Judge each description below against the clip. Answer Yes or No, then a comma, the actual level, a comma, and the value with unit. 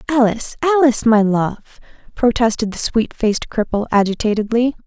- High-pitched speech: Yes, high, 230 Hz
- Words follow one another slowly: Yes, slow, 125 wpm